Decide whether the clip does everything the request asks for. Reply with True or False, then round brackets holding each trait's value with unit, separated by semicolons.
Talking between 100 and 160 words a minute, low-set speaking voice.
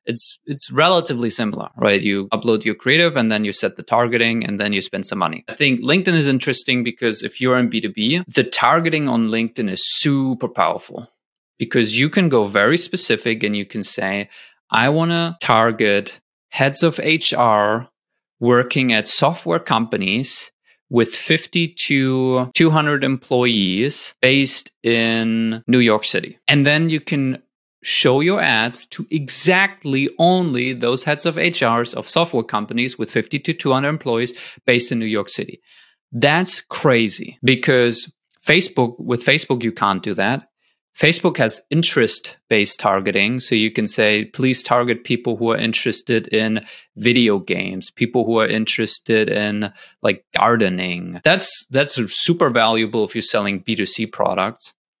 True (155 wpm; 125 Hz)